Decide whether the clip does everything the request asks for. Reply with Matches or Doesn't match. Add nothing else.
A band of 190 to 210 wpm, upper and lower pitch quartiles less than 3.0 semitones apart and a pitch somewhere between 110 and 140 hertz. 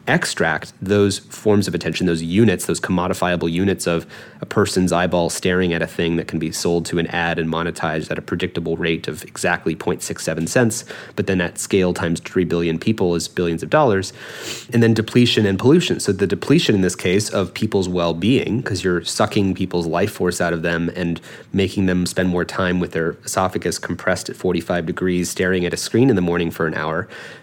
Doesn't match